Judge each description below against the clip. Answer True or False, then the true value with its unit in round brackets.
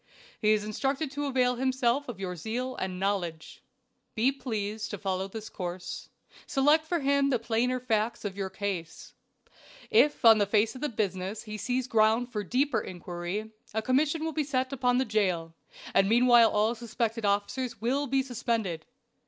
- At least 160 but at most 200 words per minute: True (170 wpm)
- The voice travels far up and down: False (4.3 semitones)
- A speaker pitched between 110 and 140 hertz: False (225 Hz)